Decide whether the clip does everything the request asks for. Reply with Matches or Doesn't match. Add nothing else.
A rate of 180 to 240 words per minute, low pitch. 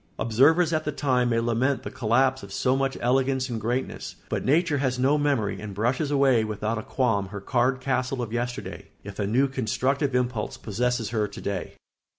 Matches